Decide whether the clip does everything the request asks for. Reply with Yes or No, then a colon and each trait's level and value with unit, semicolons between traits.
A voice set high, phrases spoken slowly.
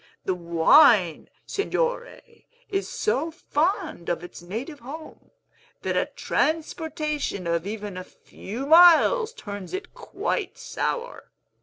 Yes: very high, 295 Hz; slow, 115 wpm